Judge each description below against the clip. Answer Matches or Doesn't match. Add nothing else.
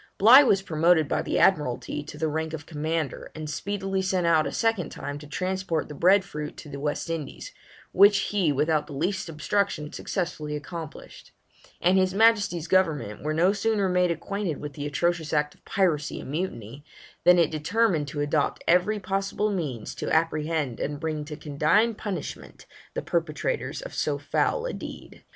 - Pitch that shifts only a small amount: Doesn't match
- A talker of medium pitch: Matches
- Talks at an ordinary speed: Matches